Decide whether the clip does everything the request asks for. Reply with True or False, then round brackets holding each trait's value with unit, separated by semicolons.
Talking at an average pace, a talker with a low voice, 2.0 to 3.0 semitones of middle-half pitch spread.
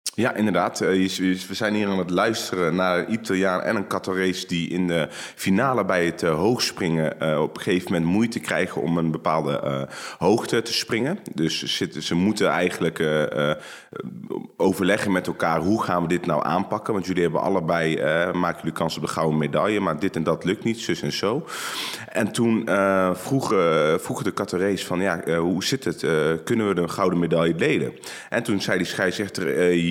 True (185 wpm; 90 Hz; 2.7 semitones)